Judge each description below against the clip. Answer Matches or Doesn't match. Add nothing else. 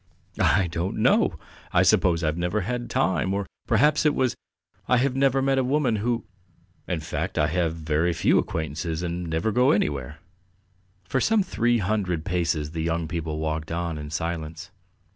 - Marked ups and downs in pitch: Matches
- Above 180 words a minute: Doesn't match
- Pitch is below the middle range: Matches